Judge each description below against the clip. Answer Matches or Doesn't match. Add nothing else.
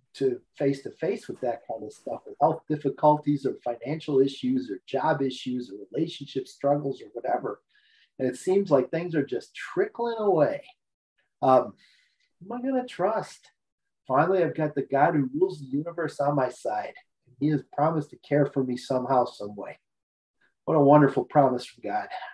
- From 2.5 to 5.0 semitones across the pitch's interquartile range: Doesn't match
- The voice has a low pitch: Doesn't match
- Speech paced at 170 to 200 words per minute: Matches